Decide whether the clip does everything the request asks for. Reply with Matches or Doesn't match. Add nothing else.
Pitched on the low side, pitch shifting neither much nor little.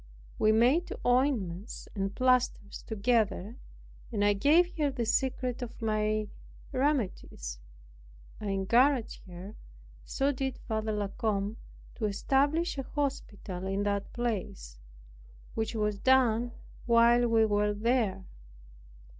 Doesn't match